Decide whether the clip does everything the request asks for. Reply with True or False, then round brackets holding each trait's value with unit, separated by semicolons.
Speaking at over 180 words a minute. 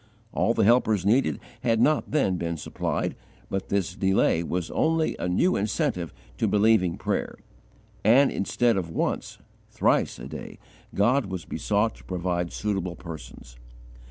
False (145 wpm)